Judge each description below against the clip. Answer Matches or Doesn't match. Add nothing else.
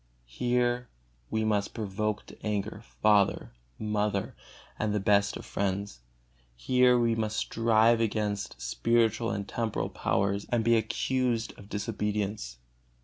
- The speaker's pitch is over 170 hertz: Doesn't match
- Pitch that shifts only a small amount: Matches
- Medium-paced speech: Doesn't match